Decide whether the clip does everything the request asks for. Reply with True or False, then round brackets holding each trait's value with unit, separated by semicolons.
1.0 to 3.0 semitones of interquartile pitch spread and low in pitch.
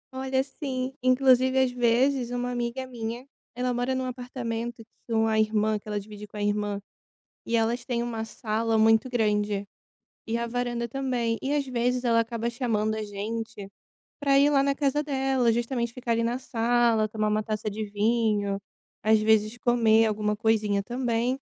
False (2.5 semitones; 235 Hz)